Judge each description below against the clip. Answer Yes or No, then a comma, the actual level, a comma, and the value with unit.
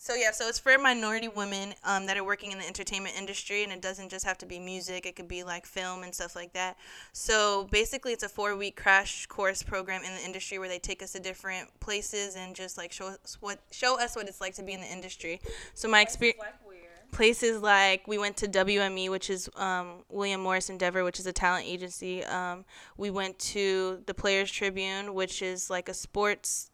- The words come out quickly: Yes, fast, 220 wpm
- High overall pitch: Yes, high, 195 Hz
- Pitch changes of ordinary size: No, narrow, 1.7 semitones